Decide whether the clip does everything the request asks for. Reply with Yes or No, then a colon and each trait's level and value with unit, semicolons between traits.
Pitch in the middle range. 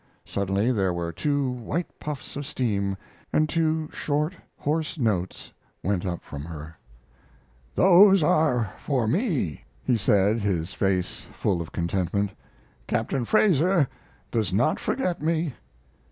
No: low, 120 Hz